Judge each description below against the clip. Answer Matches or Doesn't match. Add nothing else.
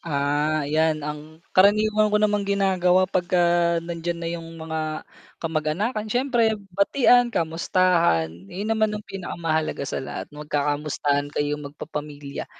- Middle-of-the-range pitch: Matches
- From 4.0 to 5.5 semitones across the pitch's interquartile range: Matches